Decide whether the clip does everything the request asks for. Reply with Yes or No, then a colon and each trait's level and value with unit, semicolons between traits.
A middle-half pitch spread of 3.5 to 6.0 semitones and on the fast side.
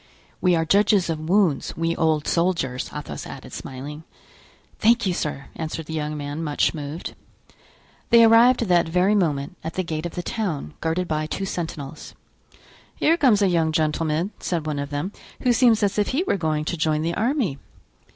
No: average, 4.5 semitones; average, 180 wpm